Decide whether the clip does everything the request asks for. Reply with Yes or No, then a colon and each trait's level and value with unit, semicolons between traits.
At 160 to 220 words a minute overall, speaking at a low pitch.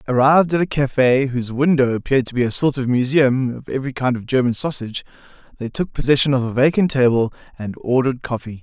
Yes: average, 200 wpm; low, 130 Hz